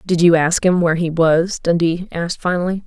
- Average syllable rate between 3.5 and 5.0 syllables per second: No, 5.5 syllables/s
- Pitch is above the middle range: No, medium, 170 Hz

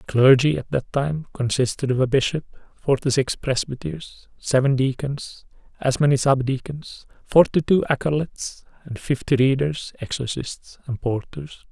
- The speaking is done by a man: Yes, male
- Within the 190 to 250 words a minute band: No, average, 140 wpm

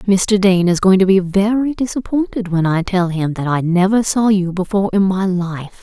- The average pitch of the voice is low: No, high, 190 Hz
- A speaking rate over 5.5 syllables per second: No, 4.9 syllables/s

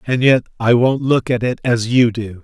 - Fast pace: Yes, fast, 245 wpm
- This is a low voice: Yes, low, 120 Hz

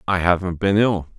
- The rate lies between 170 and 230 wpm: Yes, fast, 205 wpm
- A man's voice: Yes, male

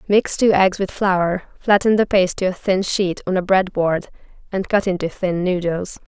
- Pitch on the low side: No, medium, 185 Hz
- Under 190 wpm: No, fast, 205 wpm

